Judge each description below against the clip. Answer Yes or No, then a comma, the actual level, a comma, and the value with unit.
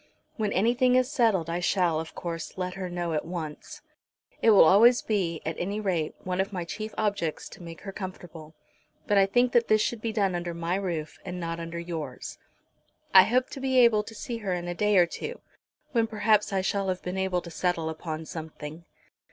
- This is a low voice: No, medium, 185 Hz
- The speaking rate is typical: No, fast, 210 wpm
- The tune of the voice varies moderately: Yes, average, 4.0 semitones